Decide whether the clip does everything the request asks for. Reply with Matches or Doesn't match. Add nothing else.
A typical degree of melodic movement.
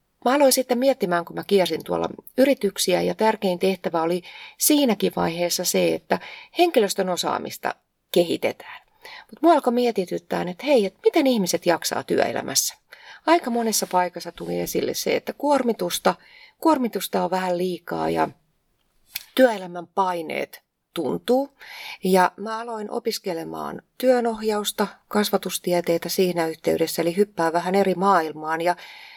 Doesn't match